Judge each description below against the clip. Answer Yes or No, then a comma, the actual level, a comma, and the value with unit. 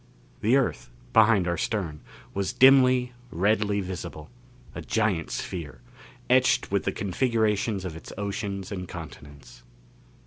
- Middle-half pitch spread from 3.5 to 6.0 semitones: Yes, average, 4.1 semitones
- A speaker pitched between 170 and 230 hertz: No, low, 100 Hz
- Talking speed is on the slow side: Yes, slow, 125 wpm